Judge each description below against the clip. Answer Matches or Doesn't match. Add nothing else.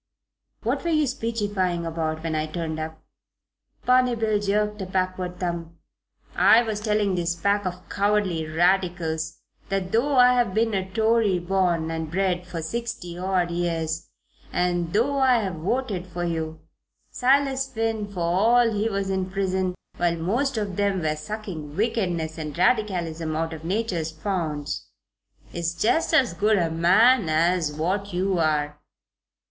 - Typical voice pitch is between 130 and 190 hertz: Matches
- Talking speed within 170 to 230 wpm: Doesn't match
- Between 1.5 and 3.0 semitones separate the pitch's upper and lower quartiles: Doesn't match